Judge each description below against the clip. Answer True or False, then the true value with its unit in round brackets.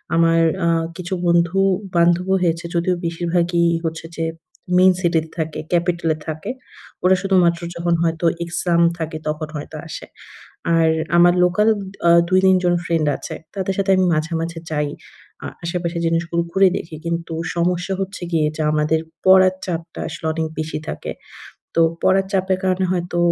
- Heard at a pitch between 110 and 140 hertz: False (170 Hz)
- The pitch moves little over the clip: True (2.0 semitones)